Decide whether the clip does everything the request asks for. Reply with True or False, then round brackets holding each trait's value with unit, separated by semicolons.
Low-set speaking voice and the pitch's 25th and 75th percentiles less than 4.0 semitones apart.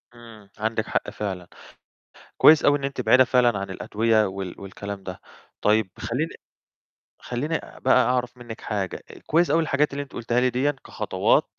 False (120 Hz; 4.4 semitones)